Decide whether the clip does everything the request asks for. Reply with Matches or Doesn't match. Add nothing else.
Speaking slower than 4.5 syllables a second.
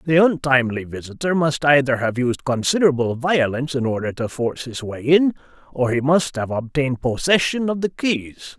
Doesn't match